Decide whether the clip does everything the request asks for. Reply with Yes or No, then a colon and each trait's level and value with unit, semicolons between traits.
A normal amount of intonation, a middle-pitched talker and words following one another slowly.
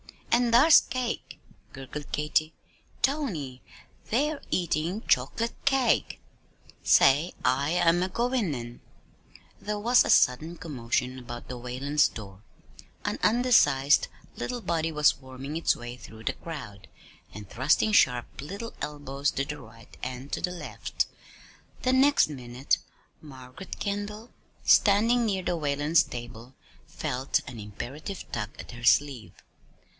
No: wide, 8.1 semitones; medium, 150 Hz; slow, 130 wpm